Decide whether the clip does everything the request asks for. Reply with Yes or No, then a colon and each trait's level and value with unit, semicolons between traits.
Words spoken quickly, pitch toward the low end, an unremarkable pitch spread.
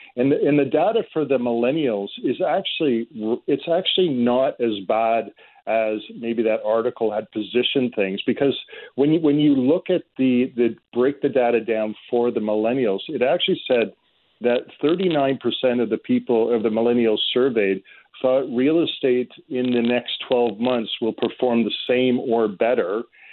No: average, 170 wpm; low, 120 Hz; average, 3.4 semitones